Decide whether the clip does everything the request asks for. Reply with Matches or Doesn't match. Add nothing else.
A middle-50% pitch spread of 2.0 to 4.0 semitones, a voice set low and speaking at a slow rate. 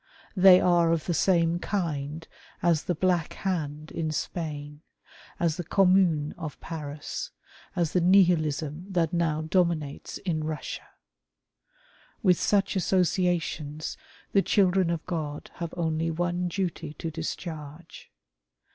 Doesn't match